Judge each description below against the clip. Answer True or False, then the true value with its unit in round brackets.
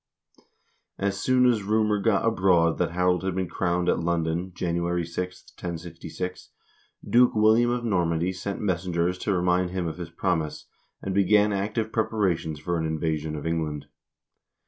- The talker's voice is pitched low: True (90 Hz)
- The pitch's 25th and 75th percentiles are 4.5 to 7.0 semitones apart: False (3.0 semitones)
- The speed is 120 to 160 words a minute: True (155 wpm)